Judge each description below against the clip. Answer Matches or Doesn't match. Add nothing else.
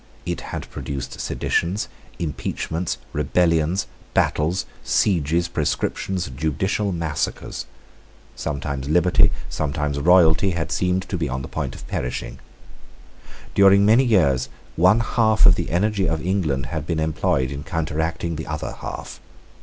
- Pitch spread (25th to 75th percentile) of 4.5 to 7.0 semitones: Doesn't match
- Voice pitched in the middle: Doesn't match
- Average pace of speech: Doesn't match